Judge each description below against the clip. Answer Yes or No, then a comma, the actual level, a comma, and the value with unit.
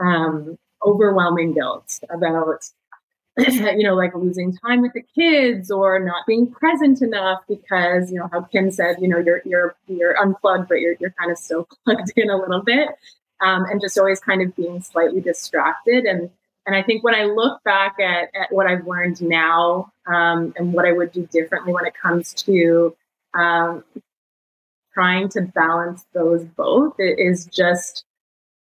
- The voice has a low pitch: No, medium, 180 Hz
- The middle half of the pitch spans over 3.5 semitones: No, average, 2.8 semitones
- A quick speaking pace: No, average, 175 wpm